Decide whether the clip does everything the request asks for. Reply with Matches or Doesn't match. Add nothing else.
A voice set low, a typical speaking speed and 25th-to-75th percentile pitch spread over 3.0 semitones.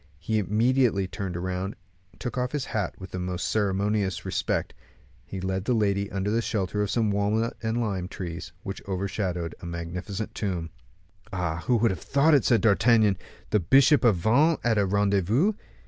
Matches